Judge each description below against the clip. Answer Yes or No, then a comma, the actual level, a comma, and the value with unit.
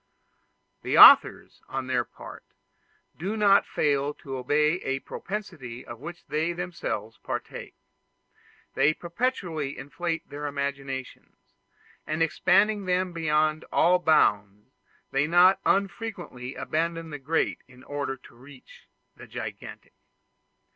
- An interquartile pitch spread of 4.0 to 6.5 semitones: Yes, average, 4.5 semitones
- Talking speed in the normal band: No, slow, 115 wpm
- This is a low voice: No, medium, 155 Hz